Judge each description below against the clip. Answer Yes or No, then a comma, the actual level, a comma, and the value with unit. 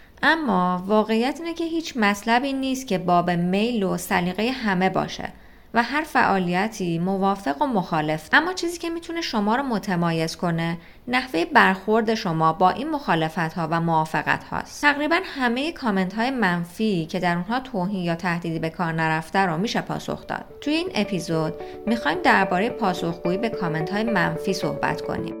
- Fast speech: Yes, fast, 160 wpm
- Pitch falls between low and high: No, high, 195 Hz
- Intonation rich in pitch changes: Yes, wide, 6.4 semitones